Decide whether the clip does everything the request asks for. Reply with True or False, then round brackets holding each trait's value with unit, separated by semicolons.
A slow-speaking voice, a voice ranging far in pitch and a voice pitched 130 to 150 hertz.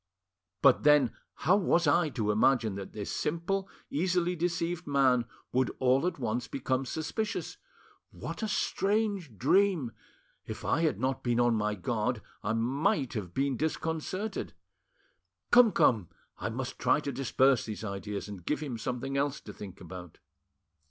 False (150 wpm; 7.0 semitones; 135 Hz)